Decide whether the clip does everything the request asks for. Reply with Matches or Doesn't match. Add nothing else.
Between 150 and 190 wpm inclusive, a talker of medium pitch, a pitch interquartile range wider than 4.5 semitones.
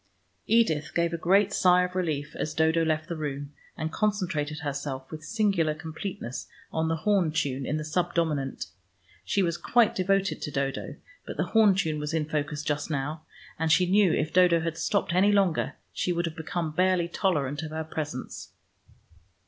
Doesn't match